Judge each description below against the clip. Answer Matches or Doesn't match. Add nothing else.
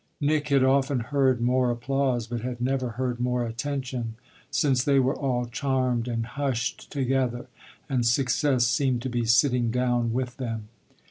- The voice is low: Matches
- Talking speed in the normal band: Matches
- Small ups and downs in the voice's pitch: Matches